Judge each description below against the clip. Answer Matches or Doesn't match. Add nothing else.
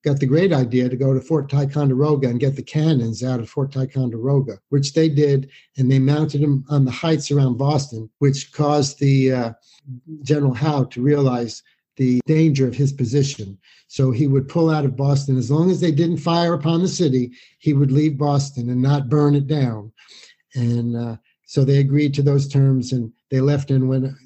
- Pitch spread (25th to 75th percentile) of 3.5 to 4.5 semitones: Doesn't match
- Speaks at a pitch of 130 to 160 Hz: Matches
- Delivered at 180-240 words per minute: Matches